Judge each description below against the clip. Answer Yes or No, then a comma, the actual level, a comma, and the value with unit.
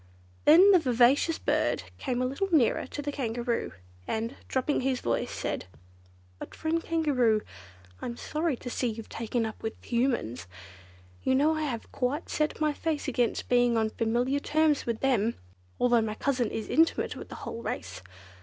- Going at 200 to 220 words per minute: No, average, 170 wpm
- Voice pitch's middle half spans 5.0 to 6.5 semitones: No, average, 4.3 semitones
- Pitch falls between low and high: No, very high, 250 Hz